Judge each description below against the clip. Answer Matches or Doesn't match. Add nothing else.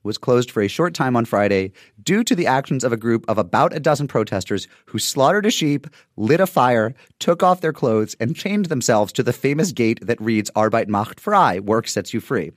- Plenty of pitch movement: Matches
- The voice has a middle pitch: Doesn't match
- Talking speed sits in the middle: Doesn't match